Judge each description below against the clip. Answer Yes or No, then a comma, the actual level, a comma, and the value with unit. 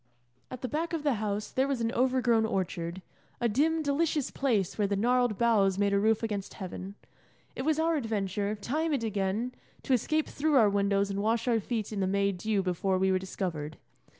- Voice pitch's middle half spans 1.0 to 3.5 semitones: No, average, 4.5 semitones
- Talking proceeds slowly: No, fast, 205 wpm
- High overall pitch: Yes, high, 220 Hz